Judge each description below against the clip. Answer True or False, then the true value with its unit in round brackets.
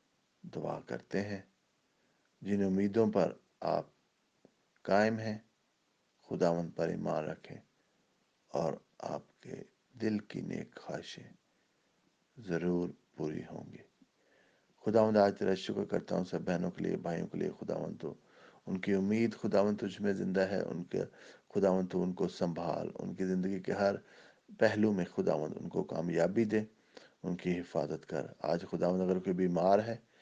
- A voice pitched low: True (95 Hz)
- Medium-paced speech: True (145 wpm)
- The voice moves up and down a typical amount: True (3.1 semitones)